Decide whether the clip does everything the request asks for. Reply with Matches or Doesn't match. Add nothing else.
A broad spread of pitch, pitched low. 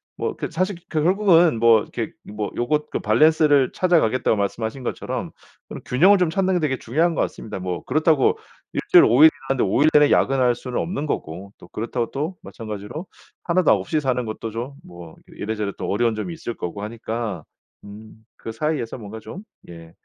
Matches